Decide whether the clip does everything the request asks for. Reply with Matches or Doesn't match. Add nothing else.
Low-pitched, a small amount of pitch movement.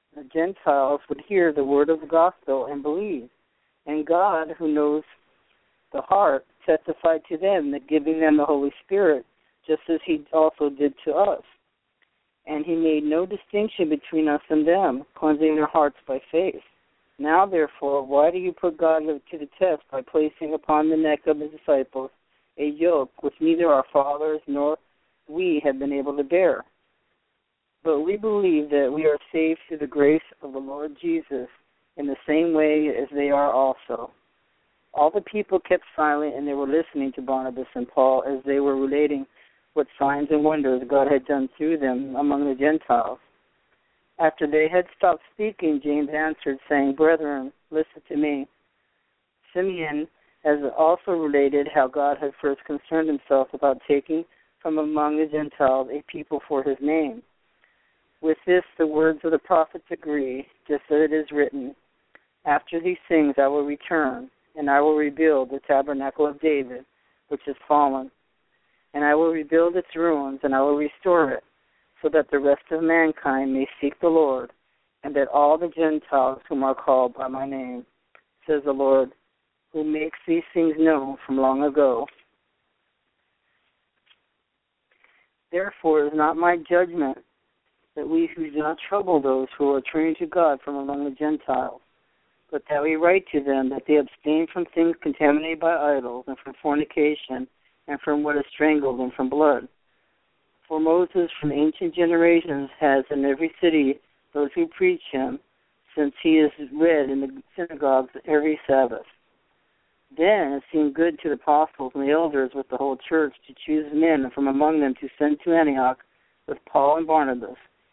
Doesn't match